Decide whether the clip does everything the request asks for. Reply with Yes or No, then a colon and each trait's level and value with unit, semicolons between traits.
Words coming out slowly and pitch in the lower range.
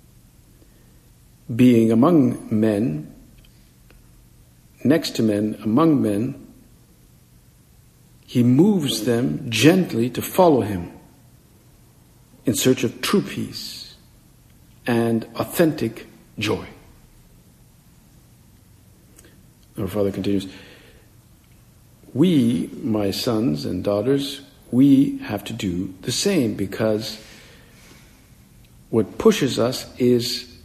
Yes: slow, 80 wpm; low, 110 Hz